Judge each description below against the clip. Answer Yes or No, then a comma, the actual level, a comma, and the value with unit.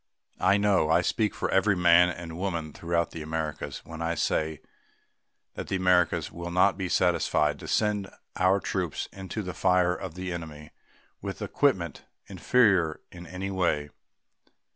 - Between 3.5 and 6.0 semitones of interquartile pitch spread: No, average, 2.7 semitones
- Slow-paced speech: No, average, 155 wpm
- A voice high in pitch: No, very low, 90 Hz